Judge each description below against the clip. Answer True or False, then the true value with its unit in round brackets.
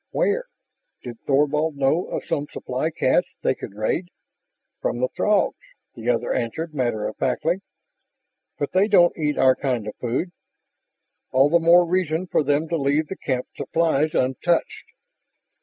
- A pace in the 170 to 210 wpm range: False (155 wpm)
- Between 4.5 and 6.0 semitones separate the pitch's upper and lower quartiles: True (4.8 semitones)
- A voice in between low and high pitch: True (150 Hz)